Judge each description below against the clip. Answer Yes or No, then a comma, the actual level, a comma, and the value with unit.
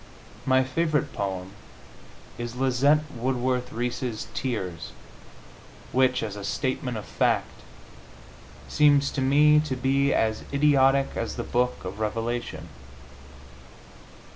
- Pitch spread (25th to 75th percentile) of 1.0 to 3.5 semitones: Yes, average, 3.2 semitones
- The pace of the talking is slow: Yes, slow, 110 wpm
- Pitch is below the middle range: Yes, low, 130 Hz